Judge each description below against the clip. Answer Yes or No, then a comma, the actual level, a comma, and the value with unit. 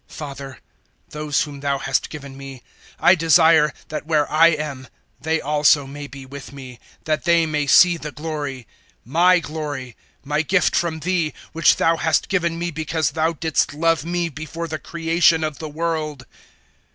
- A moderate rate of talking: Yes, average, 170 wpm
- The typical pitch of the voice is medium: Yes, medium, 155 Hz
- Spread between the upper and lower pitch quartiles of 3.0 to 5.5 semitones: No, narrow, 2.5 semitones